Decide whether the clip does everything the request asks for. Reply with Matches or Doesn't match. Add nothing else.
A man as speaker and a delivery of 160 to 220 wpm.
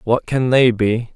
Matches